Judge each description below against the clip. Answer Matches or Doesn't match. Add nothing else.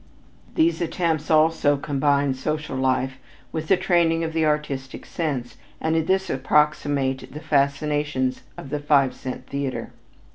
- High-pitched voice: Doesn't match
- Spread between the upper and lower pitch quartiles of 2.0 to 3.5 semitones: Matches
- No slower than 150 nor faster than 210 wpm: Doesn't match